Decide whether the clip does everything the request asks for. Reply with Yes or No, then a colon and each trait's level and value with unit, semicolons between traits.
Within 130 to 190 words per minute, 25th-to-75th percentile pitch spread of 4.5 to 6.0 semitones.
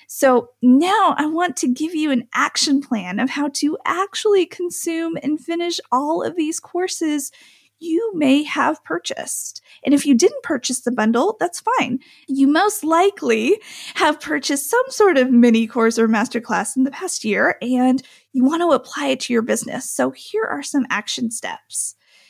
Yes: average, 175 wpm; wide, 5.5 semitones